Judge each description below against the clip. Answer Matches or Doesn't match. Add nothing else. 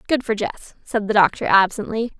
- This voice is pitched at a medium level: Doesn't match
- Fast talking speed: Doesn't match